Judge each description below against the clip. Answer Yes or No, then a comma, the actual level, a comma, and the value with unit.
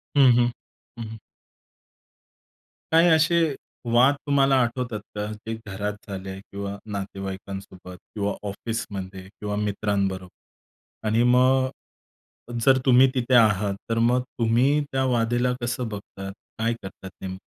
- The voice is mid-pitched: No, low, 110 Hz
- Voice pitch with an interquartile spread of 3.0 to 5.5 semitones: Yes, average, 4.0 semitones